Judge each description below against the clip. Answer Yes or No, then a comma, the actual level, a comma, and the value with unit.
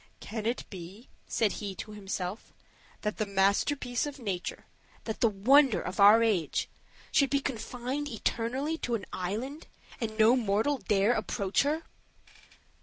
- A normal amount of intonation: Yes, average, 4.6 semitones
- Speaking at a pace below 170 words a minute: Yes, average, 150 wpm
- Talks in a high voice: Yes, high, 225 Hz